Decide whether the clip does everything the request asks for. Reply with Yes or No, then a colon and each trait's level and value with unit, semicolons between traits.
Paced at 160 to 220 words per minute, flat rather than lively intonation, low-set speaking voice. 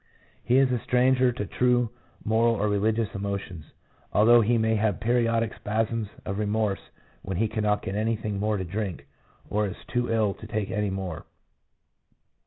Yes: average, 165 wpm; narrow, 2.1 semitones; low, 110 Hz